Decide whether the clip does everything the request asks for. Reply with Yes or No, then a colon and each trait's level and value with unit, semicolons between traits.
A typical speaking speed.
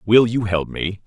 No: fast, 225 wpm